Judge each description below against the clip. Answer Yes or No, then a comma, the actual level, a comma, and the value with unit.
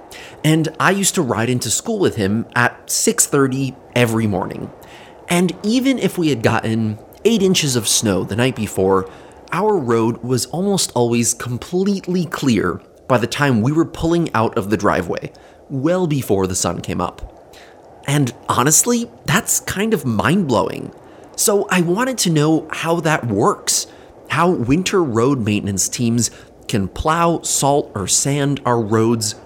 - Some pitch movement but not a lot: No, wide, 7.1 semitones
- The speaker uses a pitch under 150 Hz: Yes, low, 135 Hz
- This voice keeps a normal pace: Yes, average, 155 wpm